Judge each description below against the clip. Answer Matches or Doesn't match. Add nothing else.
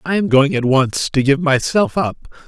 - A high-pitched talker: Doesn't match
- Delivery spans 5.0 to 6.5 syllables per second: Doesn't match